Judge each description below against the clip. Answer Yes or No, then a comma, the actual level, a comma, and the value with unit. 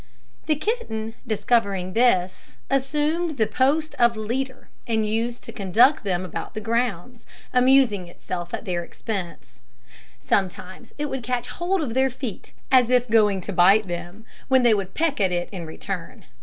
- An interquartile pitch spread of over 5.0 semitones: Yes, wide, 5.4 semitones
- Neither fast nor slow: Yes, average, 160 wpm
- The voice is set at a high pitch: Yes, high, 225 Hz